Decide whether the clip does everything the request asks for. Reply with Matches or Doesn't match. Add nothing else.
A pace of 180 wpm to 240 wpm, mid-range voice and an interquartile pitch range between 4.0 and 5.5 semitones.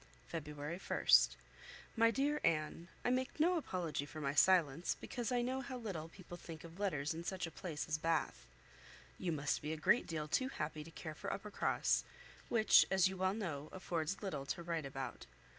Matches